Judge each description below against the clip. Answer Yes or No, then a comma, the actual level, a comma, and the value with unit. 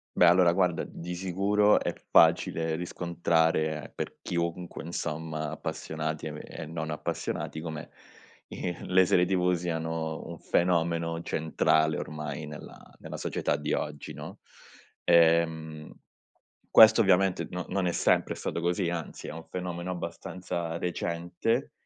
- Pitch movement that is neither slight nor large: No, narrow, 1.9 semitones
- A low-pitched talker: Yes, very low, 85 Hz